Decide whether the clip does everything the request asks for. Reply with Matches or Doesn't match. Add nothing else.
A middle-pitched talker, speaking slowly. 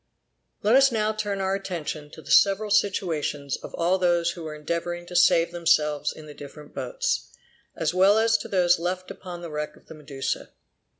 Doesn't match